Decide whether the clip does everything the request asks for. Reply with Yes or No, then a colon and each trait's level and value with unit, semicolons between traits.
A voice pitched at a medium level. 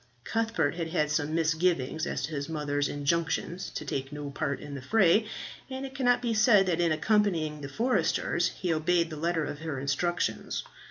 Yes: medium, 165 Hz